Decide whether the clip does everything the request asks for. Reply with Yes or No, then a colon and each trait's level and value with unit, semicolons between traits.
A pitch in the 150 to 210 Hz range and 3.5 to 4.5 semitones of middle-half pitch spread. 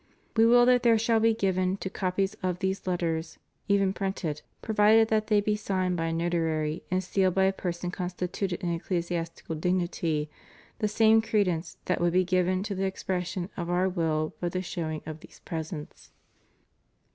No: medium, 185 Hz; average, 2.8 semitones